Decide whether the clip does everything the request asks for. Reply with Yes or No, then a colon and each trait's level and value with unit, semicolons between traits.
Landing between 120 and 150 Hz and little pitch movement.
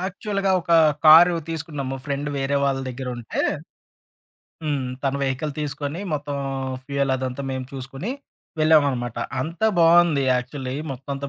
No: medium, 140 Hz; average, 3.0 semitones